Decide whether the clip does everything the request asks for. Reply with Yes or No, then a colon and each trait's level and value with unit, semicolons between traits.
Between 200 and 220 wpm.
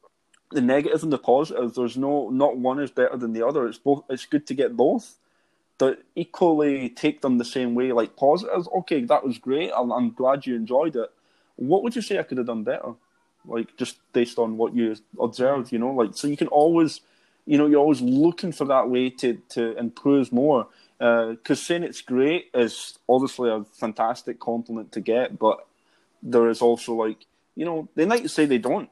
Yes: fast, 205 wpm